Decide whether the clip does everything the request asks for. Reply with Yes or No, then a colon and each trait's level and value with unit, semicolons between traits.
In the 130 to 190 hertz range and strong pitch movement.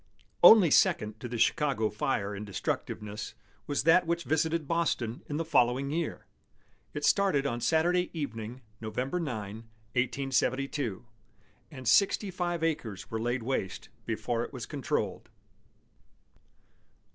Yes: low, 135 Hz; wide, 6.4 semitones